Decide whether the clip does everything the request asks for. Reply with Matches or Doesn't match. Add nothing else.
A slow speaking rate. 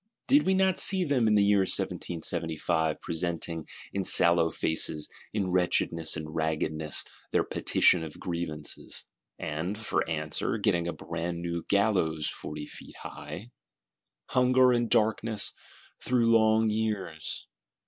Matches